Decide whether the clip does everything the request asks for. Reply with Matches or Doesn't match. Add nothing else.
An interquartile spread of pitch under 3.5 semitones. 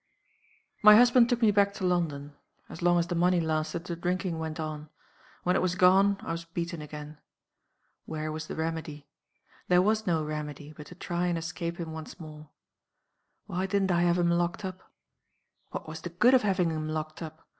Matches